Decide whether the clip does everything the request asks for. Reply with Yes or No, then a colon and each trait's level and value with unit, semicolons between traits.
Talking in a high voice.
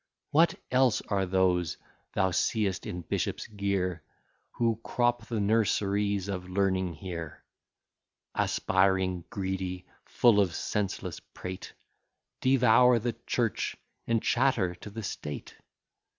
No: low, 100 Hz